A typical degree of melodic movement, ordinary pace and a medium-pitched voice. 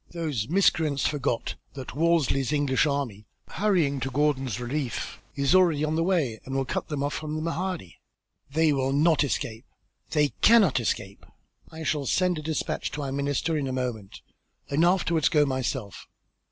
Yes: average, 3.4 semitones; average, 165 wpm; medium, 145 Hz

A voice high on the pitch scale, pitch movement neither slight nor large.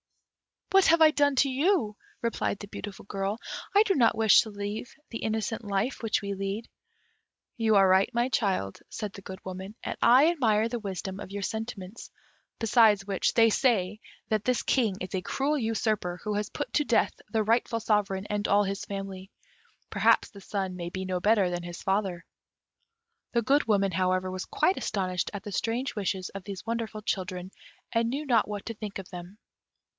Yes: high, 210 Hz; average, 3.1 semitones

